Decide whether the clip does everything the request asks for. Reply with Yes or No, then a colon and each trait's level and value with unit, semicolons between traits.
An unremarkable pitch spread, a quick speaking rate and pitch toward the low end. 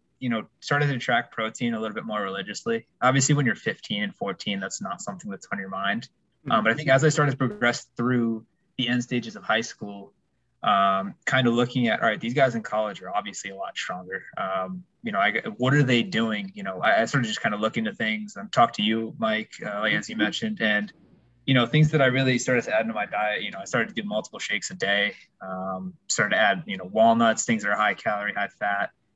No: wide, 5.8 semitones; fast, 250 wpm; low, 125 Hz